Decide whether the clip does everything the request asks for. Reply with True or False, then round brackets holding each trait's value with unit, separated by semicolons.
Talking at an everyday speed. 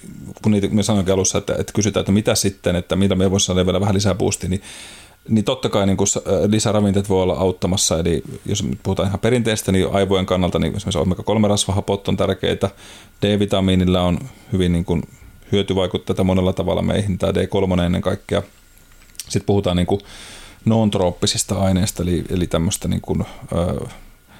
False (165 wpm)